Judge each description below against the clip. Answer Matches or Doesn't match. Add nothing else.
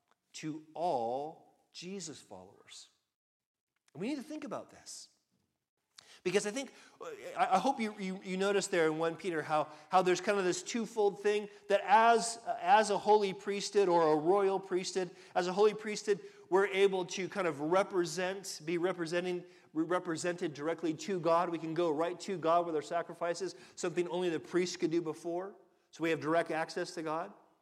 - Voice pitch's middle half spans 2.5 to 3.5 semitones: Matches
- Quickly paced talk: Doesn't match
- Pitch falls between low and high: Matches